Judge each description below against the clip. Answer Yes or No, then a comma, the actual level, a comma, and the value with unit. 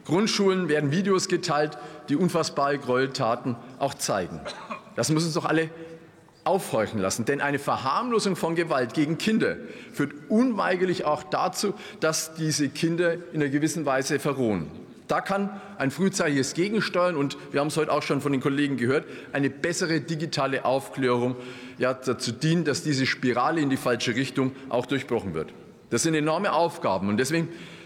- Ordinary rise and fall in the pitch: Yes, average, 4.2 semitones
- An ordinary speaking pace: Yes, average, 160 wpm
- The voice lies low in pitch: No, medium, 150 Hz